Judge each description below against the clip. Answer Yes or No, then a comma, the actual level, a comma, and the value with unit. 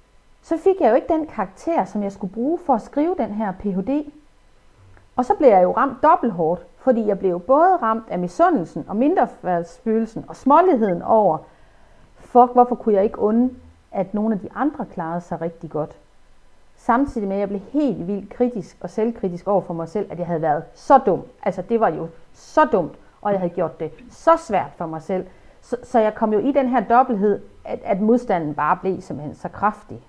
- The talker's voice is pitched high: Yes, high, 210 Hz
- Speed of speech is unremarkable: Yes, average, 210 wpm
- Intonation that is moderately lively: No, wide, 5.9 semitones